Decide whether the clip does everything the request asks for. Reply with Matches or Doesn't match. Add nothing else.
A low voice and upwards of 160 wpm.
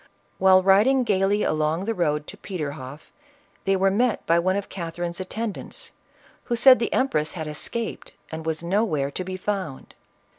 Doesn't match